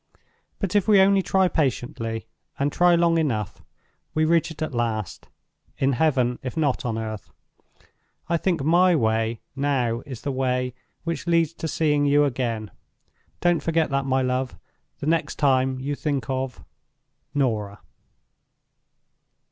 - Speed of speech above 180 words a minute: No, average, 140 wpm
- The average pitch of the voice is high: No, medium, 140 Hz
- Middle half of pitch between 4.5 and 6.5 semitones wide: Yes, average, 4.8 semitones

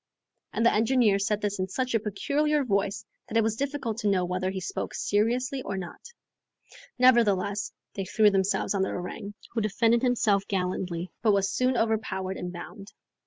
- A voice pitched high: Yes, high, 205 Hz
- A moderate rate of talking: Yes, average, 175 wpm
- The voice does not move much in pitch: No, average, 3.4 semitones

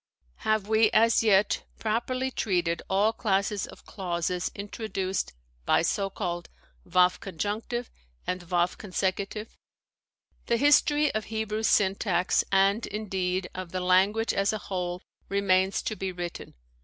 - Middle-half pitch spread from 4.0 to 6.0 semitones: No, average, 3.0 semitones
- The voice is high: Yes, high, 195 Hz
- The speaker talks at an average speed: No, slow, 130 wpm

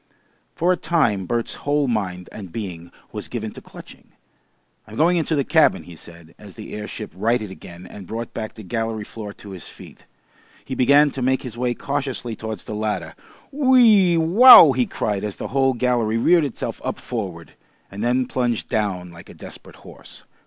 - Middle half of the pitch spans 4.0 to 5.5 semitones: Yes, average, 5.1 semitones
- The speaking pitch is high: No, low, 115 Hz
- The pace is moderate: Yes, average, 185 wpm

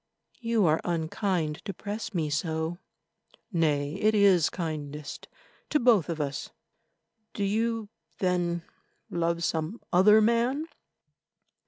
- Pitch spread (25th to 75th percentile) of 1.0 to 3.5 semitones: No, average, 5.0 semitones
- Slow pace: Yes, slow, 115 wpm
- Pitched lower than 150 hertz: No, medium, 175 Hz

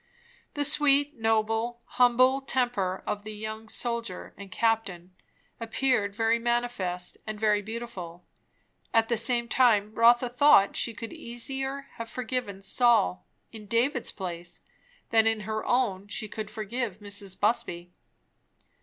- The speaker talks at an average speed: No, slow, 130 wpm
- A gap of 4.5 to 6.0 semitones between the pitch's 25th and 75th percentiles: No, average, 3.0 semitones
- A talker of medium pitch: No, high, 225 Hz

